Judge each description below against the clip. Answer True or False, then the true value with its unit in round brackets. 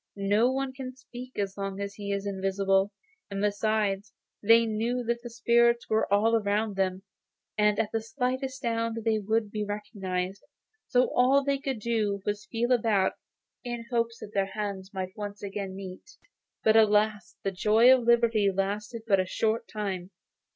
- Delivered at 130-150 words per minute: False (175 wpm)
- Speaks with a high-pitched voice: True (210 Hz)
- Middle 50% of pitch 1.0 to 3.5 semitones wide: True (2.9 semitones)